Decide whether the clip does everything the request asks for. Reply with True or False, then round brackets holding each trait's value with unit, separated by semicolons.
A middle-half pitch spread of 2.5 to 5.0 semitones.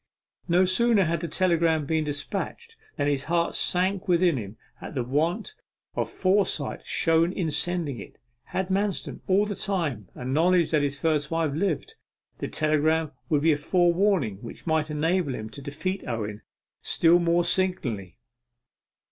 True (4.0 semitones)